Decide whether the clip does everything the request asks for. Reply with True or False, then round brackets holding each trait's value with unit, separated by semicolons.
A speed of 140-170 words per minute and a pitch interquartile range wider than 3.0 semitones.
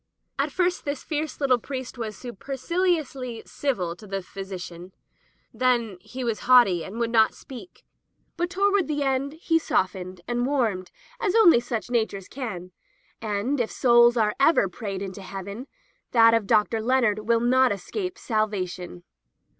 True (155 wpm; 5.4 semitones)